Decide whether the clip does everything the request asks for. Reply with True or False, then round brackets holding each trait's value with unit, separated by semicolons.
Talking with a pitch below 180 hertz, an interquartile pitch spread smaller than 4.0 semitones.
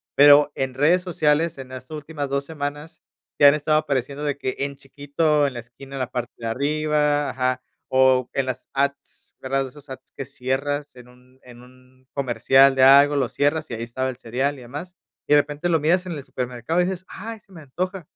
True (140 Hz; 2.6 semitones)